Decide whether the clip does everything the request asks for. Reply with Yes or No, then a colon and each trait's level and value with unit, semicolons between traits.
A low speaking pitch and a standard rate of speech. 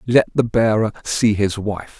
Yes: low, 110 Hz; average, 180 wpm